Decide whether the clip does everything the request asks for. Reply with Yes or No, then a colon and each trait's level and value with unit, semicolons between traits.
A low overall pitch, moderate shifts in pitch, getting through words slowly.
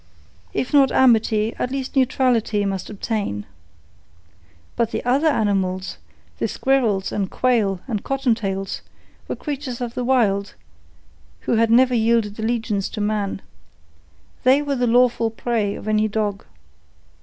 No: high, 225 Hz; average, 3.5 semitones; slow, 130 wpm